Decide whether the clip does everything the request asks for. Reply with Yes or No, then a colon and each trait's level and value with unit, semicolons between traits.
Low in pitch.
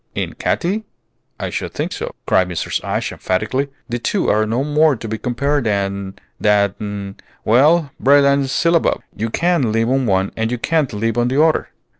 Yes: low, 120 Hz